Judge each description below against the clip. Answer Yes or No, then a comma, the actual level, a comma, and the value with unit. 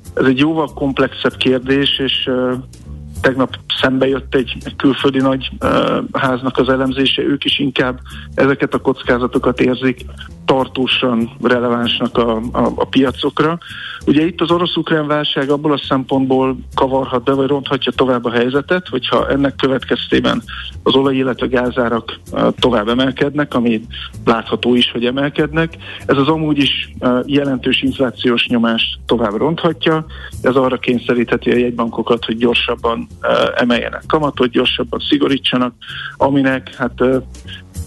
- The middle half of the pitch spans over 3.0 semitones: No, narrow, 2.6 semitones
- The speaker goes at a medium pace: Yes, average, 135 wpm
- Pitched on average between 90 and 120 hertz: No, low, 130 Hz